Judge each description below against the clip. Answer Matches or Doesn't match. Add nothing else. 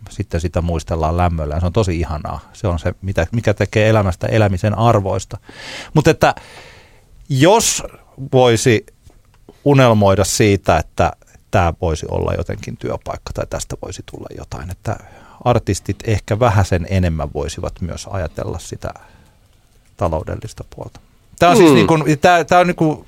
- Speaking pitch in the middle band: Doesn't match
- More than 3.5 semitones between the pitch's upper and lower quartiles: Matches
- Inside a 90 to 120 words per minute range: Doesn't match